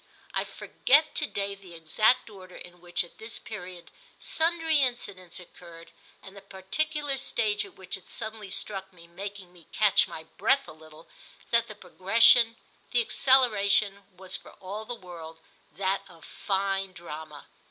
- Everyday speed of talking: Yes, average, 155 wpm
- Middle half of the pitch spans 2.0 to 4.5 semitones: Yes, average, 3.9 semitones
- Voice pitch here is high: Yes, high, 195 Hz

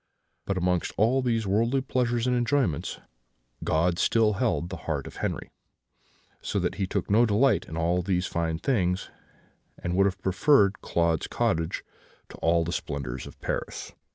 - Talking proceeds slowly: No, average, 160 wpm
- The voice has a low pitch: Yes, very low, 95 Hz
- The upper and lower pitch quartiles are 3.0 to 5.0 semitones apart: No, wide, 5.4 semitones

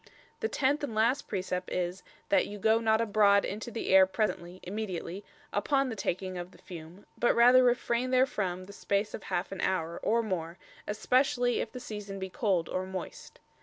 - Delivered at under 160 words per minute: No, average, 185 wpm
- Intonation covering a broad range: No, average, 4.2 semitones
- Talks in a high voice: Yes, high, 205 Hz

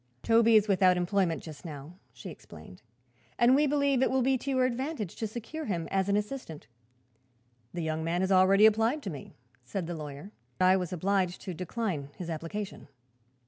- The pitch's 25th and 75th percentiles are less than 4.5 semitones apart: No, wide, 5.6 semitones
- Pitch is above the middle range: Yes, high, 195 Hz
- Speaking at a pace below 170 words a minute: No, average, 185 wpm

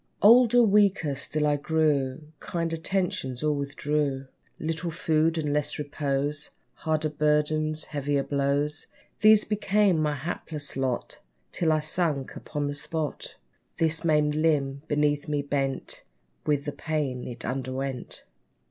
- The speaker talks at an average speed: No, slow, 130 wpm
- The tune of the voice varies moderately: No, narrow, 2.1 semitones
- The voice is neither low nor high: Yes, medium, 150 Hz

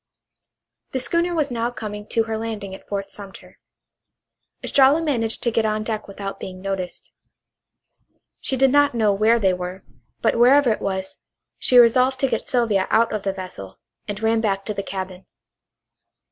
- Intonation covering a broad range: No, average, 3.7 semitones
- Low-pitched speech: No, high, 220 Hz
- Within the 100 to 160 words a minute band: No, average, 170 wpm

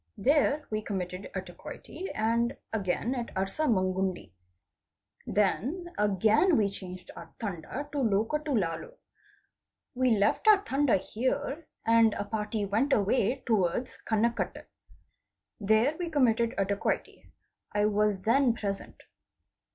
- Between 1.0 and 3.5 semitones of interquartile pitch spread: No, average, 5.1 semitones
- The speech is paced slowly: Yes, slow, 115 wpm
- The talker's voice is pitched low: No, high, 220 Hz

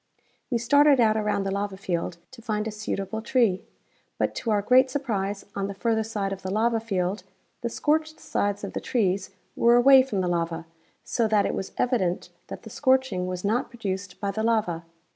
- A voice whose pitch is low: No, high, 210 Hz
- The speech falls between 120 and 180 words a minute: No, average, 200 wpm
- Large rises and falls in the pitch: No, average, 3.7 semitones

